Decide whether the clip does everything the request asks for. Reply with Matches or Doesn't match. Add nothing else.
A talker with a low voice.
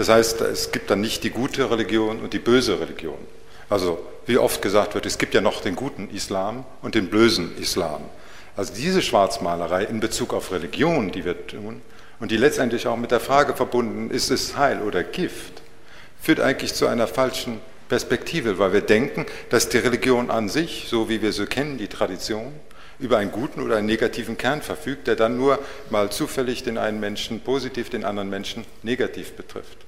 Matches